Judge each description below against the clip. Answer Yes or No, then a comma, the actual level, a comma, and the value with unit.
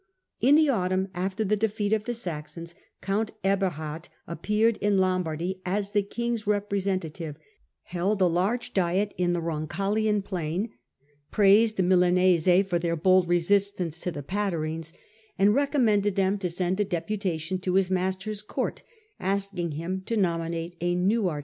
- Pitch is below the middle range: No, high, 190 Hz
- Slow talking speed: No, average, 150 wpm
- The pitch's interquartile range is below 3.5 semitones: Yes, average, 2.9 semitones